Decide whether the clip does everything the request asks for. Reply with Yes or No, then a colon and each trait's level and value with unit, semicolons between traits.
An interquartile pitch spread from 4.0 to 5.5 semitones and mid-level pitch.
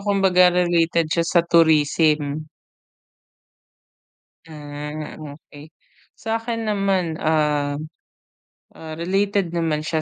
No: average, 3.4 semitones; medium, 165 Hz